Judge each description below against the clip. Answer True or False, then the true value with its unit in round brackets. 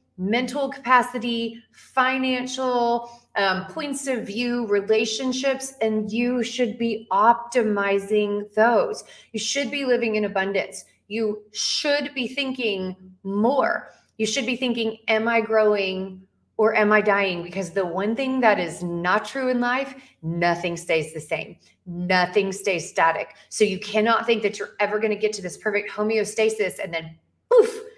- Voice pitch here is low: False (220 Hz)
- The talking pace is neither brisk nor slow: True (150 wpm)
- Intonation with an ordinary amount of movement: True (3.8 semitones)